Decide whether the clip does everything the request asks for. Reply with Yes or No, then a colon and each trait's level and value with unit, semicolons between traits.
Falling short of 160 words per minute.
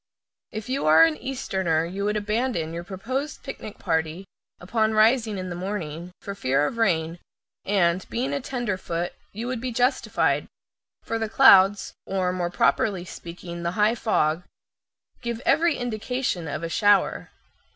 Yes: average, 150 wpm